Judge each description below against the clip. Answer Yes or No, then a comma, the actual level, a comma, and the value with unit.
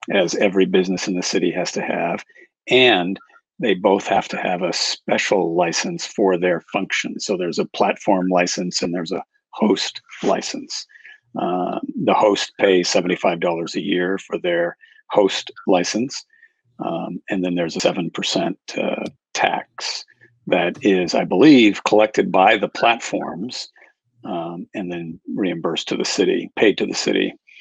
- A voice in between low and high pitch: No, low, 105 Hz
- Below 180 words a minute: Yes, average, 150 wpm